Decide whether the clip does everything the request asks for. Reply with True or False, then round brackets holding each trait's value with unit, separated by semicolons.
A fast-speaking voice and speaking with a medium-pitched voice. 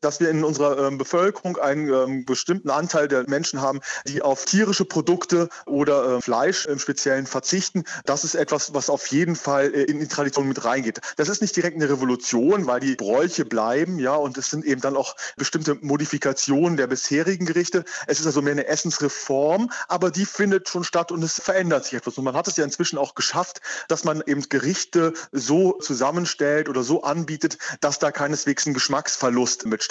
True (195 wpm; 145 Hz)